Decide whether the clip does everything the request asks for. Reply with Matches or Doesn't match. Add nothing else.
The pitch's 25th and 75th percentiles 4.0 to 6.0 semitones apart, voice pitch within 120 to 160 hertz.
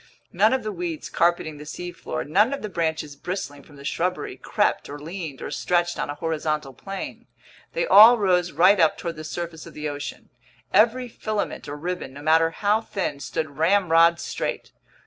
Doesn't match